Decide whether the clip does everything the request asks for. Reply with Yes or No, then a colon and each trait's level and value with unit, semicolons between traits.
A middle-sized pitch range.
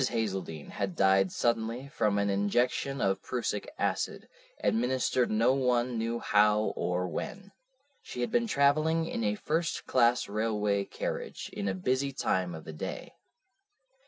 Yes: average, 4.4 semitones